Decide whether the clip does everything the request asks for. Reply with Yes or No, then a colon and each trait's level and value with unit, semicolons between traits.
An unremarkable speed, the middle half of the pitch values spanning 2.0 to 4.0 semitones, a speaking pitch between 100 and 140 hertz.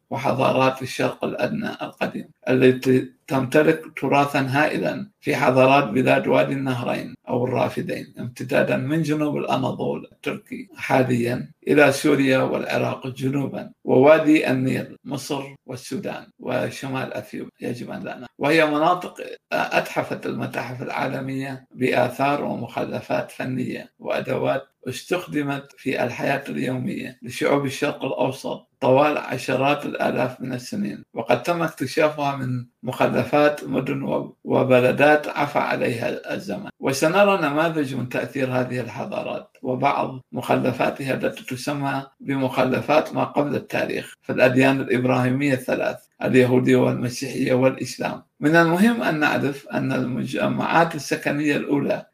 Yes: average, 110 wpm; narrow, 2.5 semitones; low, 135 Hz